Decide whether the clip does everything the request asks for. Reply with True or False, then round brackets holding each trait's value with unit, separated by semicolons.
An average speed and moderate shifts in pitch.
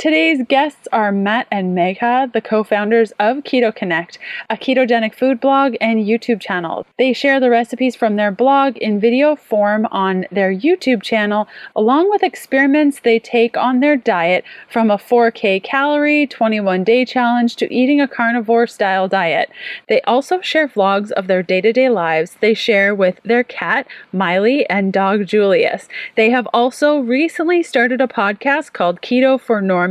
True (160 wpm; 4.3 semitones)